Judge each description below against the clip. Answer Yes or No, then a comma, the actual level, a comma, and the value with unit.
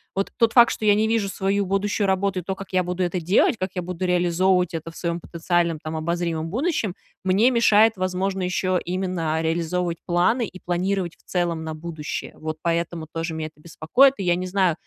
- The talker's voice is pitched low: No, medium, 180 Hz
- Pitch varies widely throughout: No, narrow, 2.6 semitones